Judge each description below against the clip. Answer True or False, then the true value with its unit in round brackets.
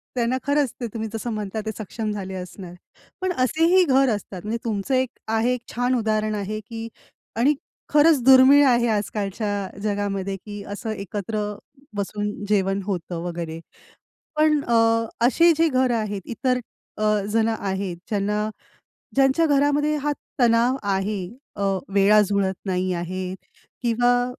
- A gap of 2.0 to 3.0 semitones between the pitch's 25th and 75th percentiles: False (4.3 semitones)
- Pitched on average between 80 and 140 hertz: False (215 Hz)